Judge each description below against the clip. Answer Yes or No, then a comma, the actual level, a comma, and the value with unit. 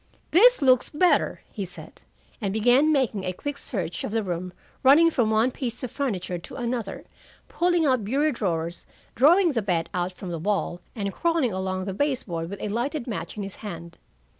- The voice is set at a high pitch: Yes, high, 220 Hz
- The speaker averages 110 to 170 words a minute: No, average, 190 wpm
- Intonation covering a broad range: Yes, wide, 6.7 semitones